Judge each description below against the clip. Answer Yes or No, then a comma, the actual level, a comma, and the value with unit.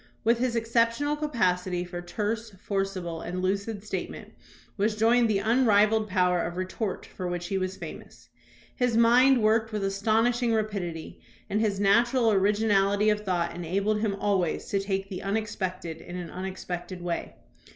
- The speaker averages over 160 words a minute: No, average, 155 wpm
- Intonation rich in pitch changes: No, average, 3.3 semitones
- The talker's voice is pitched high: Yes, high, 200 Hz